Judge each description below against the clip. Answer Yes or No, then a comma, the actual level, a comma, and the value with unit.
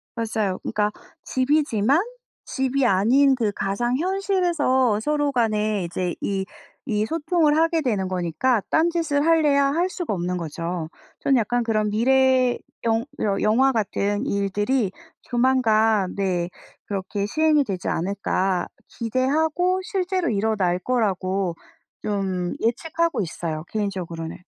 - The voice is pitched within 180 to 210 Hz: No, high, 225 Hz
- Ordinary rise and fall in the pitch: No, wide, 6.2 semitones